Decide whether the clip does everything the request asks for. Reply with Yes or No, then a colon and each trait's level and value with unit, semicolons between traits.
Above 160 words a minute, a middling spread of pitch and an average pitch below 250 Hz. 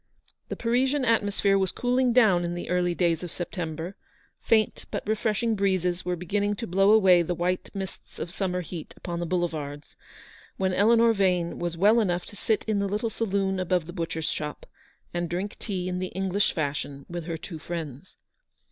Yes: average, 190 wpm; average, 3.0 semitones; medium, 185 Hz